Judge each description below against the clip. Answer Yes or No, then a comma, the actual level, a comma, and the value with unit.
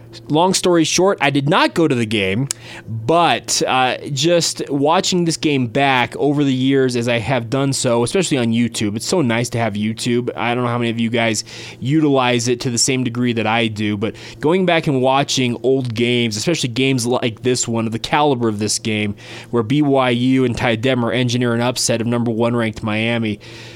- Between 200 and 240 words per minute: Yes, fast, 205 wpm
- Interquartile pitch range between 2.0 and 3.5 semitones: Yes, average, 3.0 semitones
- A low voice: Yes, low, 120 Hz